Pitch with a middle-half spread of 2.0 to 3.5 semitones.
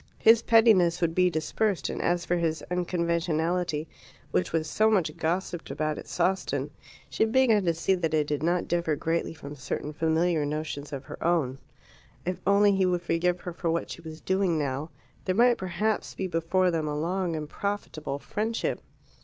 Yes: average, 3.0 semitones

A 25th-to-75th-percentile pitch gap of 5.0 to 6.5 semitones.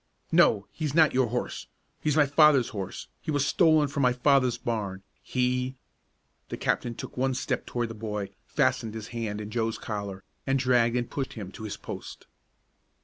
No: average, 3.9 semitones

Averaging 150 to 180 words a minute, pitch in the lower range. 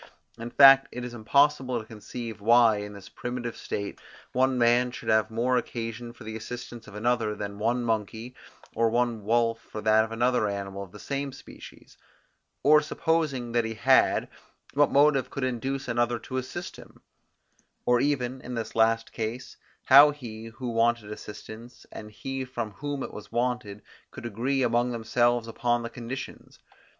Yes: average, 170 wpm; low, 120 Hz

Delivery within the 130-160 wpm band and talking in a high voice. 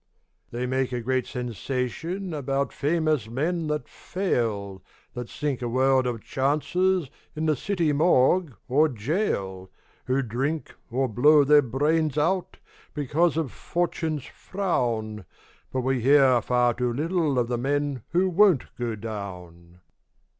No: slow, 135 wpm; low, 135 Hz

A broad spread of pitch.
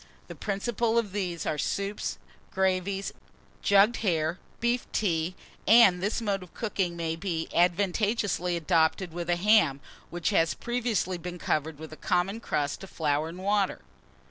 No: average, 3.5 semitones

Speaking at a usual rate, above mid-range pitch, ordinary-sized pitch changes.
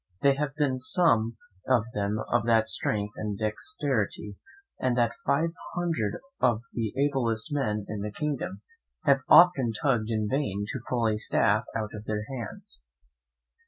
No: average, 150 wpm; low, 115 Hz; average, 4.4 semitones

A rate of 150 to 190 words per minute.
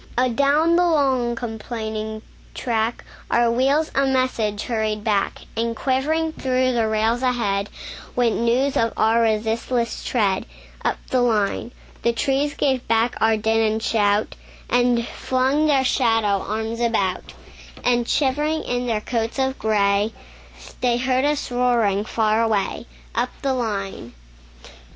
No: slow, 135 wpm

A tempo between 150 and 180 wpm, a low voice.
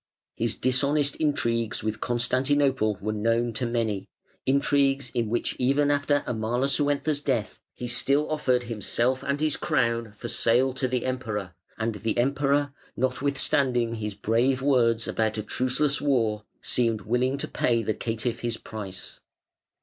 No: average, 140 wpm; low, 120 Hz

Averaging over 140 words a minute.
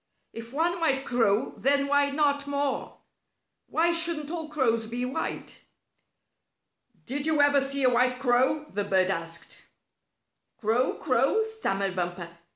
No: slow, 135 wpm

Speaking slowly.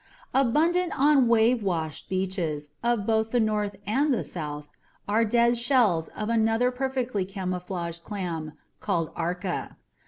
Yes: slow, 130 wpm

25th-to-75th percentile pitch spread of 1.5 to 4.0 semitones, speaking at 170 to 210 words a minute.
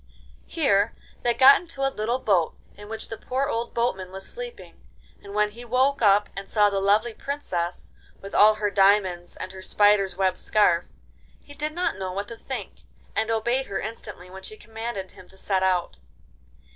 Yes: average, 3.7 semitones; average, 185 wpm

